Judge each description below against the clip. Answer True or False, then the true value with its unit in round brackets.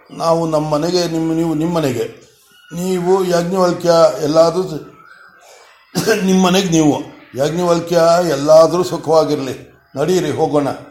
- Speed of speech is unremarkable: True (90 wpm)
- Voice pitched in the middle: True (165 Hz)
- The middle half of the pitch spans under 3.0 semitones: True (2.6 semitones)